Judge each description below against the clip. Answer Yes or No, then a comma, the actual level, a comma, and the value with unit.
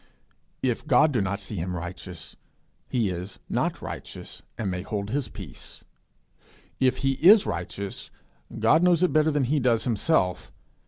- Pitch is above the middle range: No, low, 110 Hz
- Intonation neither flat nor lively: No, wide, 7.5 semitones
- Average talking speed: Yes, average, 155 wpm